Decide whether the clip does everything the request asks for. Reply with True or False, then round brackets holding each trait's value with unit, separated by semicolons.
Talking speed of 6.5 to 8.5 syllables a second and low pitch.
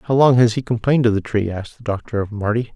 True (6.7 syllables/s; 115 Hz)